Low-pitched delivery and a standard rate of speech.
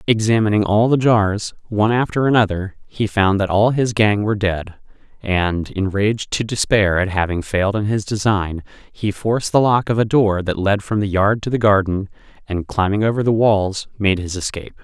Yes: low, 105 Hz; average, 195 wpm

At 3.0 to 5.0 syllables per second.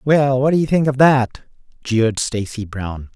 Yes: 4.5 syllables/s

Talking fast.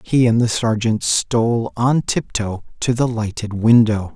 No: average, 160 wpm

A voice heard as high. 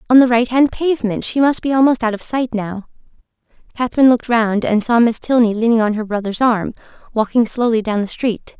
Yes: high, 235 Hz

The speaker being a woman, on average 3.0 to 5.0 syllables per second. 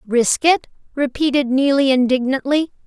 Yes: female; 4.6 syllables/s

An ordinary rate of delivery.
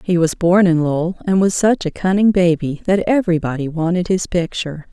Yes: average, 195 wpm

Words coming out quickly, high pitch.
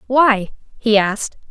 No: slow, 120 wpm; high, 225 Hz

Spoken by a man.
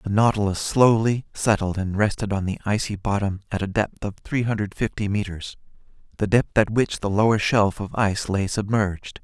Yes: male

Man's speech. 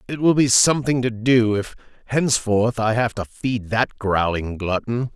Yes: male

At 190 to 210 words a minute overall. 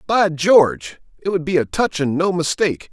Yes: fast, 205 wpm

